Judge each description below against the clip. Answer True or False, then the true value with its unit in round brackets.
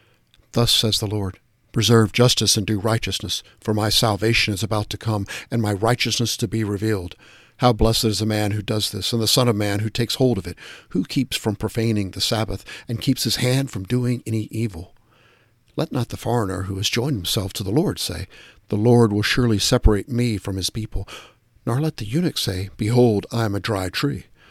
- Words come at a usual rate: False (210 wpm)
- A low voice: True (110 Hz)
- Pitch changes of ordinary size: False (2.2 semitones)